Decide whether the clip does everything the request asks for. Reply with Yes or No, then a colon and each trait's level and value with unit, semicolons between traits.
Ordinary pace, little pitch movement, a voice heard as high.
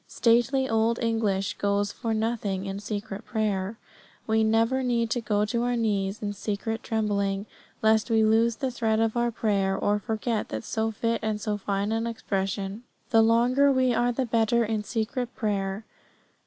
Yes: average, 170 wpm; narrow, 2.1 semitones; high, 220 Hz